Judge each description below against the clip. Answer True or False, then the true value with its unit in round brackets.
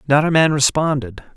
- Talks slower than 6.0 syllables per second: True (5.4 syllables/s)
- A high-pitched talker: False (145 Hz)